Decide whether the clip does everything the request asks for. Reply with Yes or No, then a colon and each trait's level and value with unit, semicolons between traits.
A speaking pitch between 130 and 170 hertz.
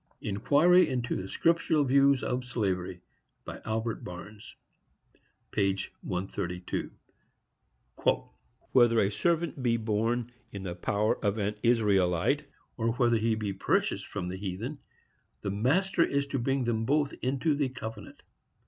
No: low, 115 Hz